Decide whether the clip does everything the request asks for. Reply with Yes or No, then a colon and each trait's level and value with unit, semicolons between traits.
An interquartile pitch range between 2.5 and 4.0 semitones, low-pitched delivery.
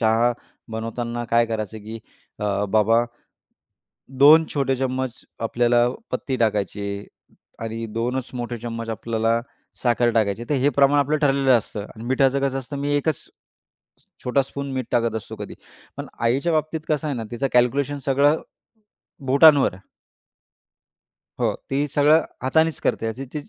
Yes: average, 3.5 semitones; low, 125 Hz